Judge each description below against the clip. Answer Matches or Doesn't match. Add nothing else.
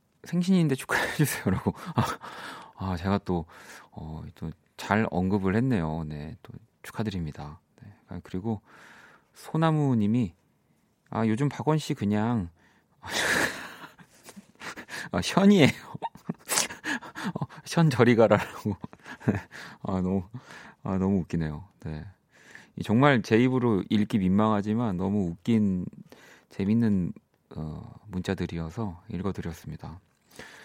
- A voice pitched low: Matches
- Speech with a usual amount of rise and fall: Matches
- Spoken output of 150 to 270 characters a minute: Matches